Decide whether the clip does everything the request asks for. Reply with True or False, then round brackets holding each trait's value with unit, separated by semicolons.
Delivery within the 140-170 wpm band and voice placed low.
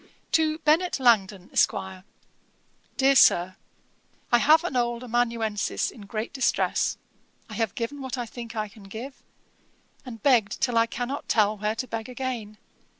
False (150 wpm; 235 Hz)